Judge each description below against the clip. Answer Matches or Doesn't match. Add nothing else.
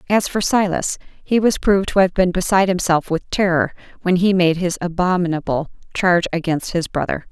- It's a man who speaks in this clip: Doesn't match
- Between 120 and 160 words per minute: Doesn't match